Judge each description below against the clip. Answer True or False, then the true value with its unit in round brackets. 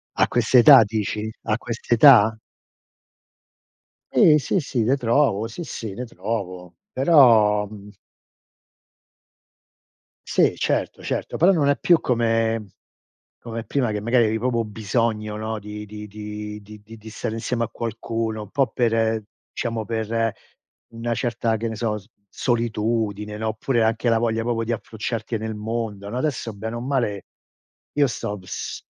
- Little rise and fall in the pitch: True (1.9 semitones)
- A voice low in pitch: True (115 Hz)